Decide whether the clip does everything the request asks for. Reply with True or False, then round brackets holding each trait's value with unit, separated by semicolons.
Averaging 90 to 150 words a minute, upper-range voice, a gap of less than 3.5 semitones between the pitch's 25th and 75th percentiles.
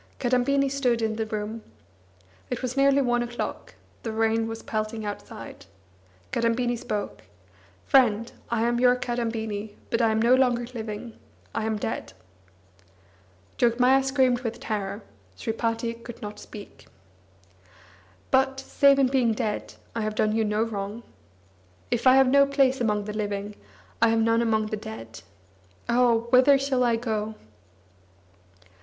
True (140 wpm; 230 Hz; 2.5 semitones)